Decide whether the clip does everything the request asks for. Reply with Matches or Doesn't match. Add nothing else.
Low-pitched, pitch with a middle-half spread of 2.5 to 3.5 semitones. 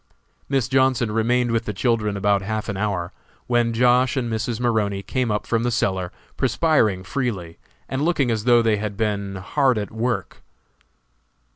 Matches